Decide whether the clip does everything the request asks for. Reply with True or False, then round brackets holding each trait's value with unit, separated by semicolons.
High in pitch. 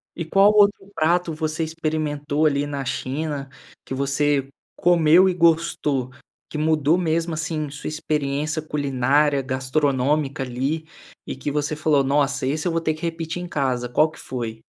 False (150 Hz)